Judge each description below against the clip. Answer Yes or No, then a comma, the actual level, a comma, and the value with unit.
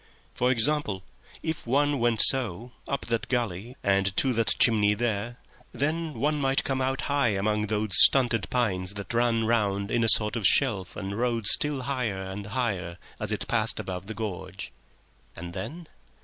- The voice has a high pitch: No, low, 115 Hz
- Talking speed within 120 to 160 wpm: No, average, 170 wpm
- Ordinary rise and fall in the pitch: Yes, average, 4.5 semitones